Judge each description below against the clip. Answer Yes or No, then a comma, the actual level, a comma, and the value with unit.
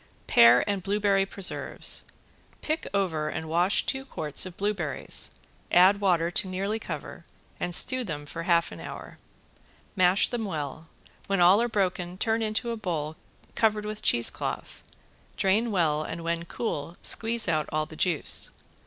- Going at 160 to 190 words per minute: No, average, 150 wpm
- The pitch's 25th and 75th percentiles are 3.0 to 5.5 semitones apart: Yes, average, 4.3 semitones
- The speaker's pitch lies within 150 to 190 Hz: Yes, medium, 185 Hz